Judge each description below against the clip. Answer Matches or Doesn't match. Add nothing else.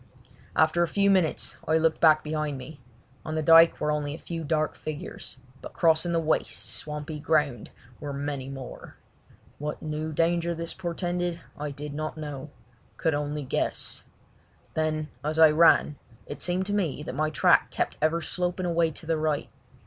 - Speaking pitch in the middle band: Matches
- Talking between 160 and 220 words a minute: Matches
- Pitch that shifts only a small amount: Matches